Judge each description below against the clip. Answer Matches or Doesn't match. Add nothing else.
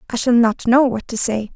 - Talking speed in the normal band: Doesn't match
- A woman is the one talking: Matches